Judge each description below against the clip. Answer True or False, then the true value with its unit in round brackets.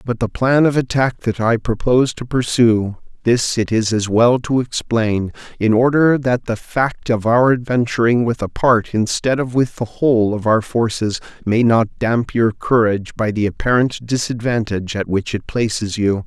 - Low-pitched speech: True (115 Hz)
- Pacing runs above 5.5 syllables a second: False (4.6 syllables/s)